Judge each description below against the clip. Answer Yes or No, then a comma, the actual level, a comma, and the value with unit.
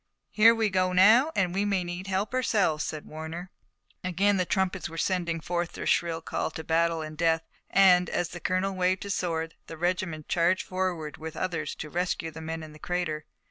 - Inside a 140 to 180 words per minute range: No, average, 200 wpm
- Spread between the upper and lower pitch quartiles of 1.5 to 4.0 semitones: Yes, narrow, 2.6 semitones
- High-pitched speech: No, medium, 175 Hz